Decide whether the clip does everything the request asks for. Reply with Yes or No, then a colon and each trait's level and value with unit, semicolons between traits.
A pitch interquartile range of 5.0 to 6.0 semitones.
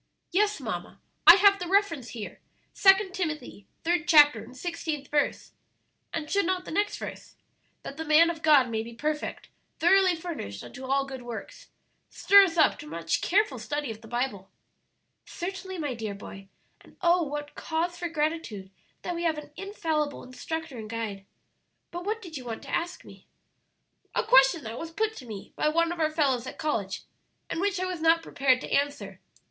Yes: wide, 5.5 semitones